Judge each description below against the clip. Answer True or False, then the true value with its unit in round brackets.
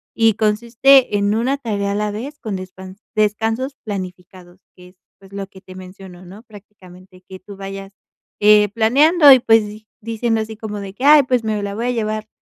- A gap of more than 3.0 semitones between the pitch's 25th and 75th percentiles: False (2.7 semitones)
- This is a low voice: False (210 Hz)